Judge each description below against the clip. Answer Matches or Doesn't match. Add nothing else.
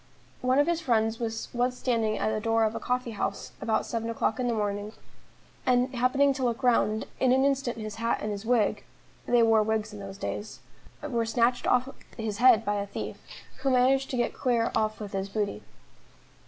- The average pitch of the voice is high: Matches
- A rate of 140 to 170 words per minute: Doesn't match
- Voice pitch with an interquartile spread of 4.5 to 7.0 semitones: Doesn't match